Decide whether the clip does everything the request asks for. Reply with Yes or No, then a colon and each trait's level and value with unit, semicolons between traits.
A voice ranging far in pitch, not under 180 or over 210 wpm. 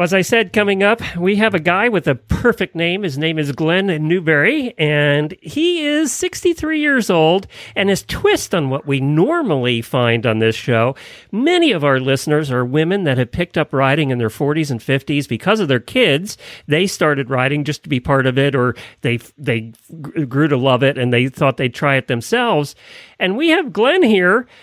Yes: wide, 6.0 semitones; average, 200 wpm